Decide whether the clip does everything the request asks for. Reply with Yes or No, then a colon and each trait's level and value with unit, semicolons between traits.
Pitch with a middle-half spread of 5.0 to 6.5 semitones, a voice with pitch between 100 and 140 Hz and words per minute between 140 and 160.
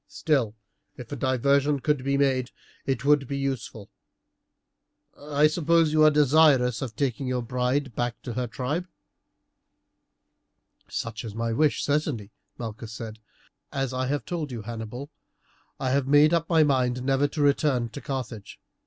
No: average, 3.2 semitones; low, 135 Hz; average, 155 wpm